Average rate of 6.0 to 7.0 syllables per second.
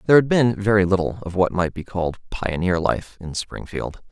No: 5.4 syllables/s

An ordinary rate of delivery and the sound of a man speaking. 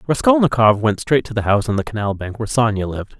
No: fast, 245 wpm; male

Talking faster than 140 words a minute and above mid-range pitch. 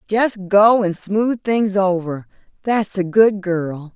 No: slow, 135 wpm; high, 195 Hz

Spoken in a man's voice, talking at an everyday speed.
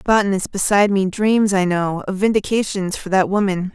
No: female; average, 190 wpm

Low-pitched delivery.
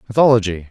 Yes: low, 110 Hz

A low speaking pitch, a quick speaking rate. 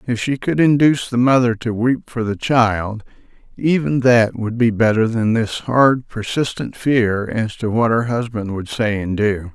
No: low, 115 Hz; average, 190 wpm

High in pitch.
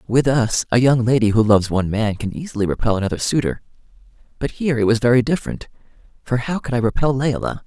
No: low, 120 Hz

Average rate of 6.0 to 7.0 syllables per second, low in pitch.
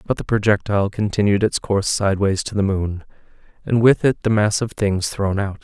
No: 5.5 syllables/s; low, 105 Hz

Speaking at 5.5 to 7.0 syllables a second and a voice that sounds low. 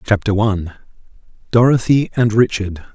No: 5.0 syllables/s; low, 110 Hz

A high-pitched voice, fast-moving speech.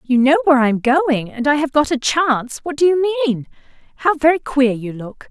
Yes: very high, 275 Hz; fast, 225 wpm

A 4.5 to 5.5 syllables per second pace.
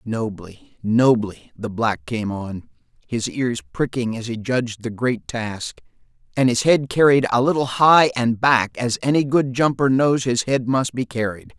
No: 4.2 syllables/s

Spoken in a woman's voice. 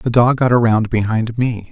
No: male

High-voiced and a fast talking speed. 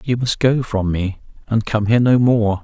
No: low, 115 Hz; fast, 225 wpm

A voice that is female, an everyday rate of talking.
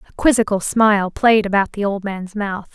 Yes: female; average, 195 wpm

